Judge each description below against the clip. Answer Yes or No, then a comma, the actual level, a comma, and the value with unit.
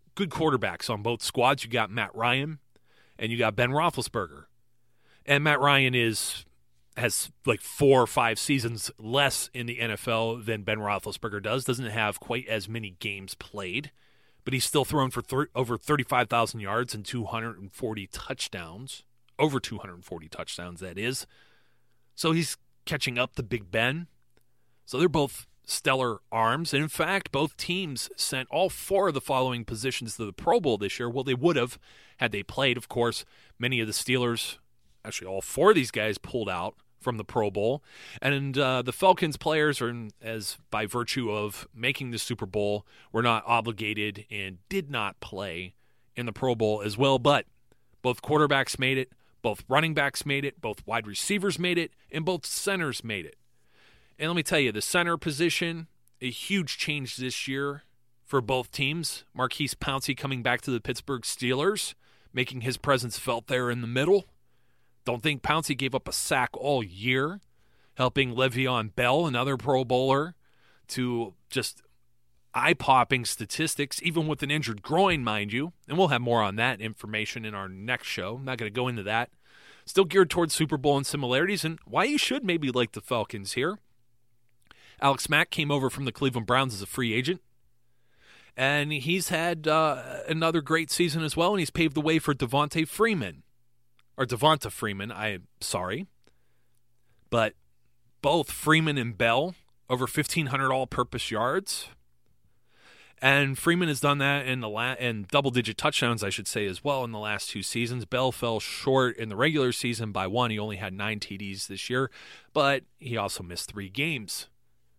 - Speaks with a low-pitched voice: Yes, low, 125 Hz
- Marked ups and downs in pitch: No, average, 4.1 semitones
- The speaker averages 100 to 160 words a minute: No, average, 175 wpm